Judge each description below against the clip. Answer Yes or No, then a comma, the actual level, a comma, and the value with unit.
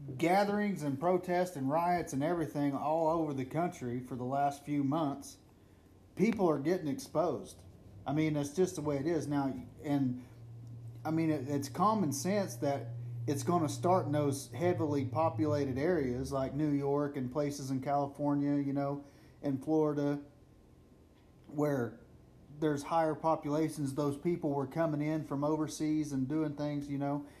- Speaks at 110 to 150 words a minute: No, average, 160 wpm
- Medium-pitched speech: Yes, medium, 145 Hz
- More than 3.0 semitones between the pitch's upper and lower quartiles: No, narrow, 2.4 semitones